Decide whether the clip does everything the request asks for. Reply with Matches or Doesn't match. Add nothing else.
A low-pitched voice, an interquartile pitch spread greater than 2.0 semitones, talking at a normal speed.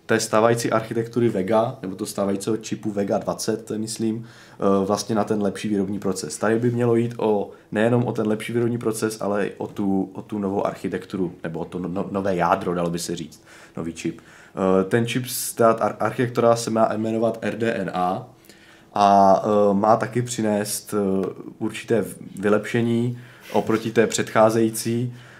Matches